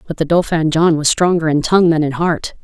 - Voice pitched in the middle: Yes, medium, 160 Hz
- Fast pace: Yes, fast, 250 wpm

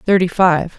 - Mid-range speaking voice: Yes, medium, 175 Hz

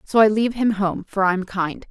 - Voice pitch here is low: No, high, 205 Hz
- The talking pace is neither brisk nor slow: No, fast, 285 wpm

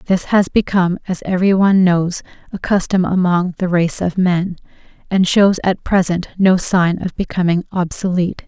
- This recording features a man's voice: No, female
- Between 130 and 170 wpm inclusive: Yes, average, 165 wpm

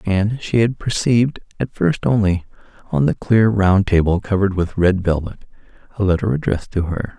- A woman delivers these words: No, male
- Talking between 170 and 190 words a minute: Yes, average, 175 wpm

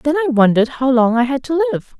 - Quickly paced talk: Yes, fast, 270 wpm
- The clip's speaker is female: Yes, female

